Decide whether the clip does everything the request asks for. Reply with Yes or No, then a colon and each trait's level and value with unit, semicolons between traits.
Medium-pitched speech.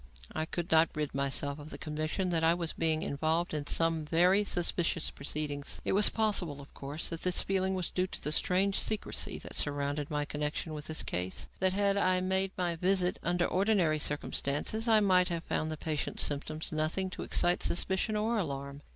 Yes: medium, 165 Hz